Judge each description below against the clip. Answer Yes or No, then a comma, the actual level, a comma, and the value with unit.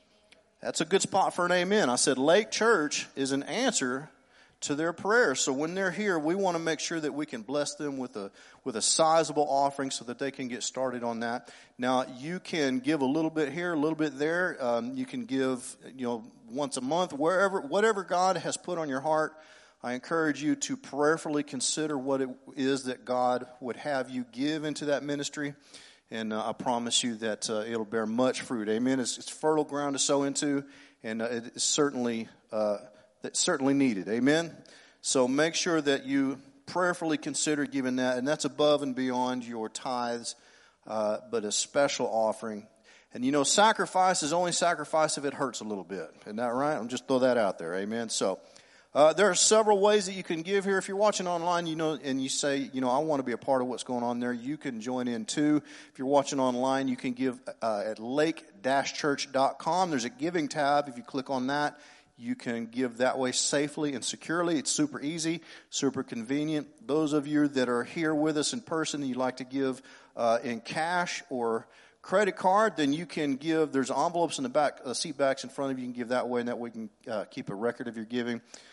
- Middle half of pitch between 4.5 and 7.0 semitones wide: No, average, 4.1 semitones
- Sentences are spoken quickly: Yes, fast, 220 wpm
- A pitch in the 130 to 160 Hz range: Yes, medium, 140 Hz